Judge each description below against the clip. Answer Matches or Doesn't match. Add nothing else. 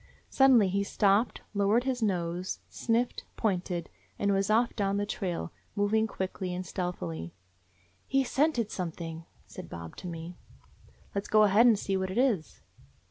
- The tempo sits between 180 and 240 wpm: Doesn't match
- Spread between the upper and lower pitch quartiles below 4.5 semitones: Matches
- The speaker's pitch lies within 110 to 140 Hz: Doesn't match